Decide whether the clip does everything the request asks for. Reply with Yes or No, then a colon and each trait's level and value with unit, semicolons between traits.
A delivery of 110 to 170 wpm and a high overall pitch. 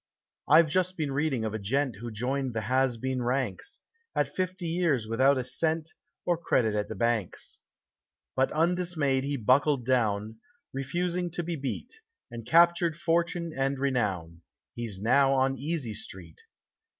No: average, 150 wpm; low, 135 Hz